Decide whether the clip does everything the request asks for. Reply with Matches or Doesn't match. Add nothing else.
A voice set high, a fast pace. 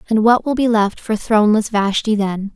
Matches